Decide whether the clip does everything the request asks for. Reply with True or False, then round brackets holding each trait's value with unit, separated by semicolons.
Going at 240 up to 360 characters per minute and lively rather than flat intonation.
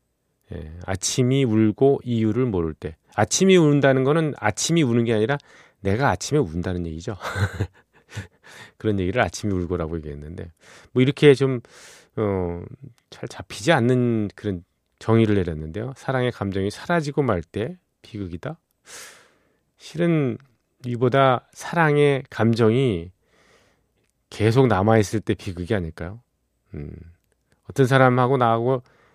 True (270 characters per minute; 5.9 semitones)